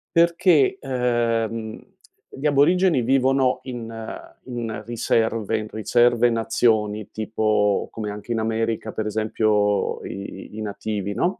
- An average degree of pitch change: No, narrow, 2.3 semitones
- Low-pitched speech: Yes, low, 115 Hz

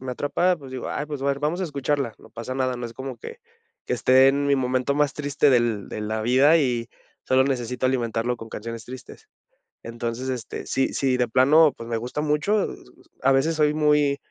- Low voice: Yes, low, 130 Hz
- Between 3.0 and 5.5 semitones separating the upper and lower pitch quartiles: Yes, average, 3.3 semitones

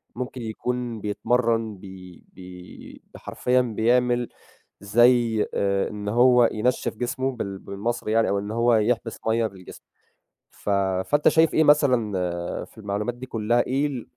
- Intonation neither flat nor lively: Yes, average, 3.0 semitones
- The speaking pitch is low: Yes, low, 115 Hz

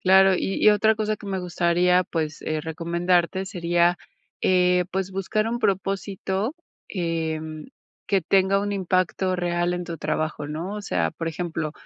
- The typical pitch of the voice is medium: Yes, medium, 180 Hz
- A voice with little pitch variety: Yes, narrow, 2.3 semitones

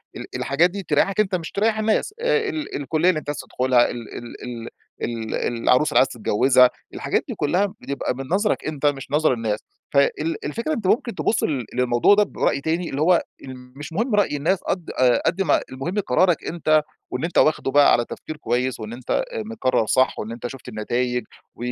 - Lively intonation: Yes, wide, 6.7 semitones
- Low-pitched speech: No, medium, 150 Hz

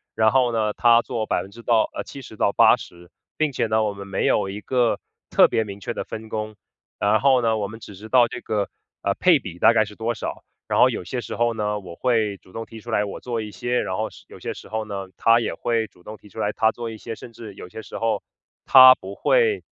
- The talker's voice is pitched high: No, low, 110 Hz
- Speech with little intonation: Yes, narrow, 2.3 semitones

